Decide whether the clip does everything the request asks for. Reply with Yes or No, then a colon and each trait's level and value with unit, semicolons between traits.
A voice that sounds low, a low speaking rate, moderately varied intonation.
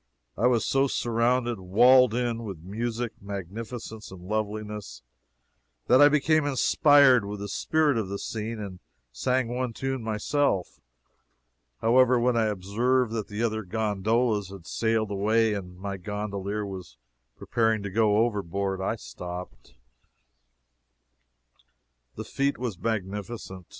Yes: low, 110 Hz; slow, 130 wpm; average, 3.4 semitones